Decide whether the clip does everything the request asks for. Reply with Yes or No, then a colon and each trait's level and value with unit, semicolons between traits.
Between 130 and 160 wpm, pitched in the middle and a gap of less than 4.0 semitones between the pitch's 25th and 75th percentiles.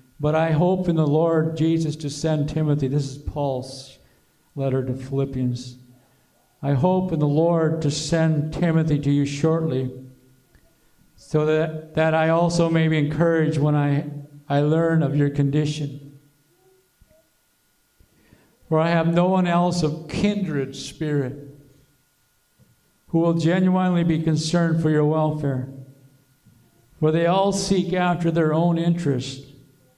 Yes: slow, 135 wpm; medium, 155 Hz; average, 2.8 semitones